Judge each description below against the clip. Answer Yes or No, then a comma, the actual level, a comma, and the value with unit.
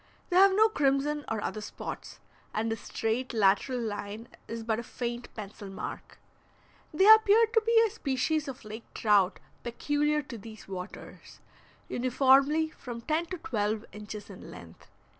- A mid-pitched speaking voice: No, high, 245 Hz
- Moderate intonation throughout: No, wide, 5.8 semitones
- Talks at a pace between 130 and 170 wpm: Yes, average, 155 wpm